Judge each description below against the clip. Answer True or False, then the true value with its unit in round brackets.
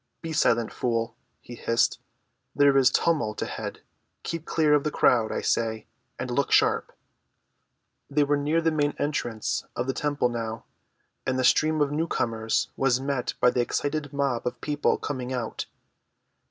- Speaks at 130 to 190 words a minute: True (160 wpm)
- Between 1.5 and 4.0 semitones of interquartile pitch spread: True (3.6 semitones)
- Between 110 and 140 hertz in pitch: True (135 Hz)